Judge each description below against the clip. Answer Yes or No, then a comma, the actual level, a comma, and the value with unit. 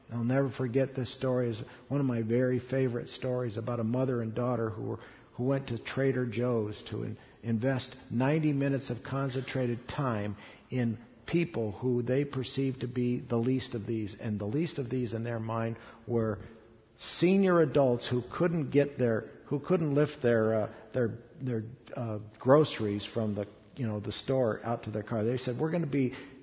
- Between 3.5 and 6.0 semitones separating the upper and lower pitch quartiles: No, average, 2.7 semitones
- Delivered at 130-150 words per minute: No, average, 190 wpm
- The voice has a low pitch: Yes, low, 125 Hz